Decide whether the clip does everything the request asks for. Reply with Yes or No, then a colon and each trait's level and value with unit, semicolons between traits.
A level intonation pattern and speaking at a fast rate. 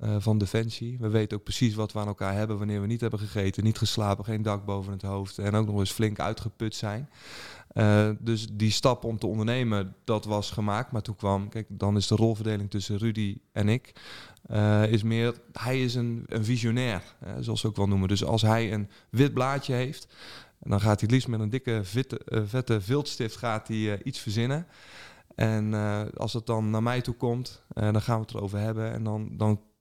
Yes: narrow, 2.0 semitones; fast, 215 wpm